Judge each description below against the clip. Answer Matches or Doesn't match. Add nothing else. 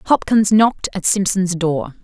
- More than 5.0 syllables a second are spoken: Doesn't match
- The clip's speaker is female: Matches